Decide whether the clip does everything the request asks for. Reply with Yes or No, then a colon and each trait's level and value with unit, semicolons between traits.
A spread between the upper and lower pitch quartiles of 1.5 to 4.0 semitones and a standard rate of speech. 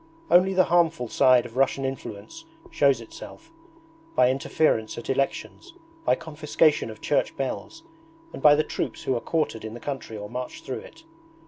No: average, 5.2 semitones; average, 165 wpm